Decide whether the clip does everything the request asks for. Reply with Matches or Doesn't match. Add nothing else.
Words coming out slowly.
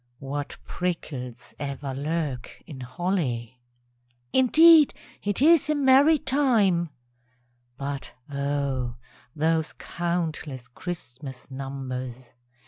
Matches